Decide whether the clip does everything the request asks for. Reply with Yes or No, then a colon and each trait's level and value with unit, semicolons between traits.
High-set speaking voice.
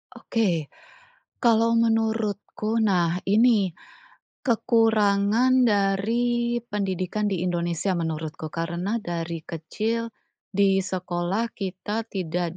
Yes: high, 200 Hz